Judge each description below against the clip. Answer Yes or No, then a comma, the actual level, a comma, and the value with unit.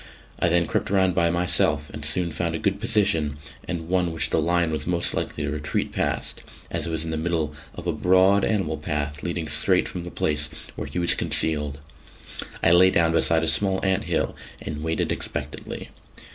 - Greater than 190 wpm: Yes, average, 200 wpm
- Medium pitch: No, very low, 85 Hz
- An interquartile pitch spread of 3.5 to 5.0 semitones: No, average, 2.8 semitones